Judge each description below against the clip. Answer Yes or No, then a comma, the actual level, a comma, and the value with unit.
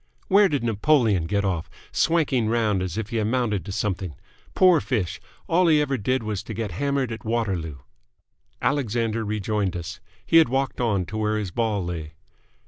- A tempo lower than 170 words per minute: No, average, 175 wpm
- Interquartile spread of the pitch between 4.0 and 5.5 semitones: Yes, average, 4.9 semitones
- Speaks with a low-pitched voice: Yes, low, 110 Hz